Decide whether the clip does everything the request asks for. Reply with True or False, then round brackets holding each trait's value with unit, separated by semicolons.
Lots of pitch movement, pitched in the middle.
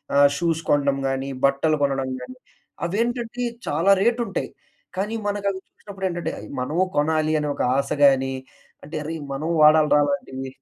True (6.0 semitones; 160 Hz)